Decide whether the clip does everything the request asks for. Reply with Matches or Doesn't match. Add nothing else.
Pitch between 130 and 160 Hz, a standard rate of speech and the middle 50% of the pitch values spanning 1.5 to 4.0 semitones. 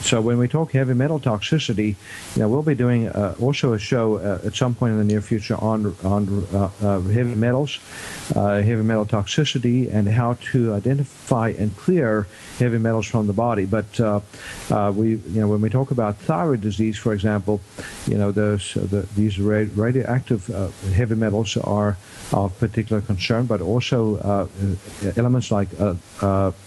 Doesn't match